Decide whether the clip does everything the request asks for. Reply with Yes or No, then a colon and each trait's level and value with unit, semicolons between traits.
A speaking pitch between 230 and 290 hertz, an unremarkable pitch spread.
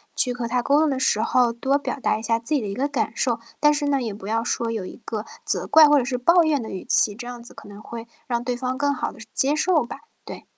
Yes: high, 245 Hz; average, 3.7 semitones